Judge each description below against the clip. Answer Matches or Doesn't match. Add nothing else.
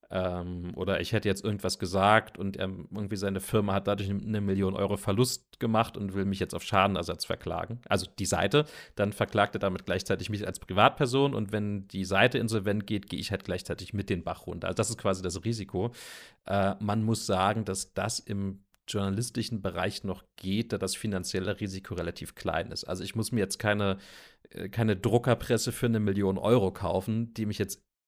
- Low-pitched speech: Matches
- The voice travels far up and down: Doesn't match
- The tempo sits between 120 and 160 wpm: Doesn't match